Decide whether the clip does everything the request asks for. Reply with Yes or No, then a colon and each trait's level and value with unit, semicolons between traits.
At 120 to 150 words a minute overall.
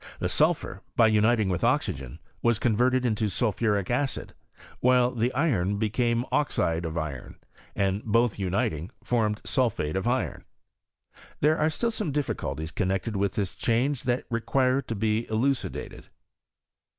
Yes: average, 140 wpm